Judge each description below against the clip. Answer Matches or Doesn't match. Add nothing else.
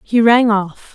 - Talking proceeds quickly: Doesn't match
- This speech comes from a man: Doesn't match